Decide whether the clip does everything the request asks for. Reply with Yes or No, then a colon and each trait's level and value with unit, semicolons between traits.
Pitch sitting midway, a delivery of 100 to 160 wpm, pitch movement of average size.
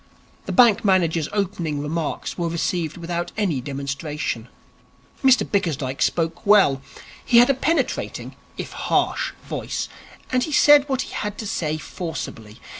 No: medium, 170 Hz; average, 140 wpm; wide, 5.9 semitones